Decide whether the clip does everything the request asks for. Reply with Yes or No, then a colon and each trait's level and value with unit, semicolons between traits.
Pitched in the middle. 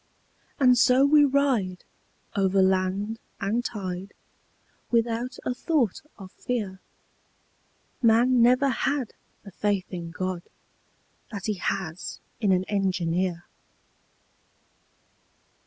No: high, 205 Hz